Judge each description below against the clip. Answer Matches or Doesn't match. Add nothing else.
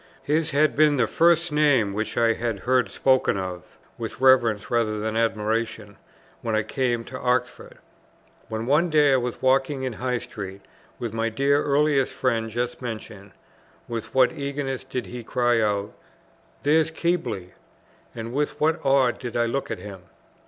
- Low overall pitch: Matches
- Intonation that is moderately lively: Matches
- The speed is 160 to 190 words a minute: Matches